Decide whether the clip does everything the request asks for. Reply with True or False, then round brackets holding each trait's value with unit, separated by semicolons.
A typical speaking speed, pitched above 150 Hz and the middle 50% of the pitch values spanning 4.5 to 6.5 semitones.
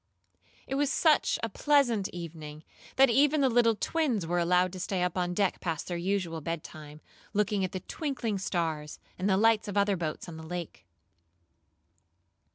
True (170 wpm; 190 Hz; 5.2 semitones)